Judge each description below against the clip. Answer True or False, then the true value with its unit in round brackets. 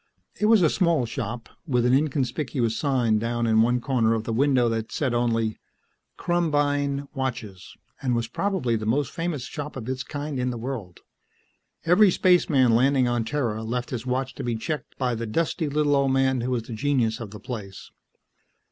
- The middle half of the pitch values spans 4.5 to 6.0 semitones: False (3.8 semitones)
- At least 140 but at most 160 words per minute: False (185 wpm)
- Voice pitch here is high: False (125 Hz)